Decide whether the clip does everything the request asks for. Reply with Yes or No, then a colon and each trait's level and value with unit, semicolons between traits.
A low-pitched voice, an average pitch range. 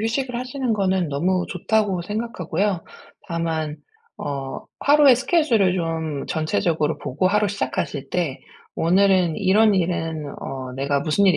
No: medium, 180 Hz; average, 5.0 semitones